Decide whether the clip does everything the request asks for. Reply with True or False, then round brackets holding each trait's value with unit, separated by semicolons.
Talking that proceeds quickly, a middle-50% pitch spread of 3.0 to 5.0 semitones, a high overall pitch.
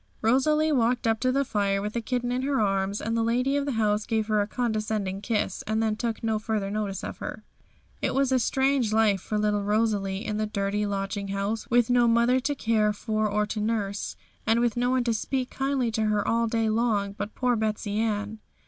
False (220 wpm; 2.6 semitones; 220 Hz)